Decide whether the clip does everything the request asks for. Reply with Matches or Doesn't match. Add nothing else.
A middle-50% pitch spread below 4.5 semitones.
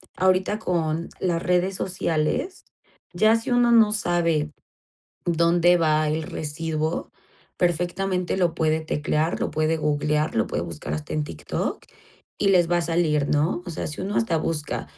Matches